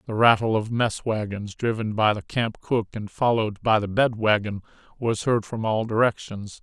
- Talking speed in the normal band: Yes, average, 190 wpm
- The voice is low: Yes, low, 110 Hz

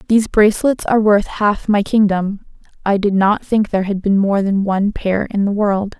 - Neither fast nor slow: No, fast, 210 wpm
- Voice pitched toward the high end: Yes, high, 205 Hz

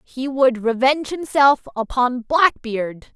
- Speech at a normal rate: No, slow, 115 wpm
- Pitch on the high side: Yes, very high, 260 Hz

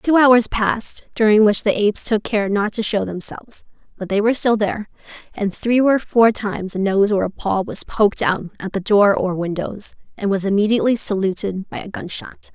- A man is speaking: No, female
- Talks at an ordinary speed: No, fast, 210 wpm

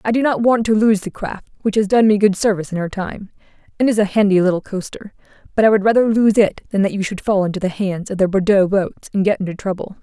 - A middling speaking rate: No, fast, 270 wpm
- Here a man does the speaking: No, female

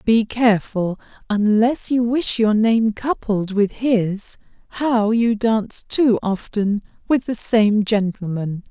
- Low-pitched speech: No, high, 220 Hz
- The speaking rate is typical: No, slow, 130 wpm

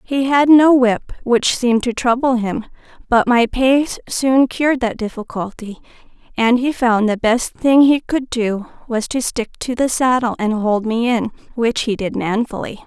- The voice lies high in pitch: Yes, high, 240 Hz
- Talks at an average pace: Yes, average, 180 wpm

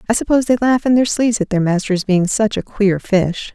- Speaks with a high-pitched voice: Yes, high, 210 Hz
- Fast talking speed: Yes, fast, 255 wpm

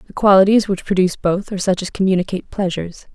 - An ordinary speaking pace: Yes, average, 190 wpm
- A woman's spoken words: Yes, female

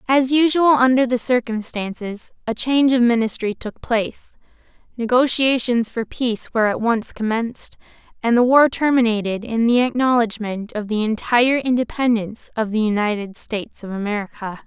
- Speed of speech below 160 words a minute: Yes, average, 145 wpm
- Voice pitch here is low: No, high, 235 Hz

